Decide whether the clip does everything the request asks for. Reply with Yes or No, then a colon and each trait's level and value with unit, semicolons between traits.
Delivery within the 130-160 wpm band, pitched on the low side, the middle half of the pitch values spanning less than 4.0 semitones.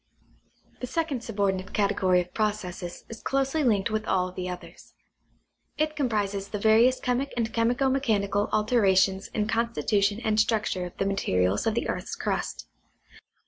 No: average, 150 wpm; high, 215 Hz; average, 3.4 semitones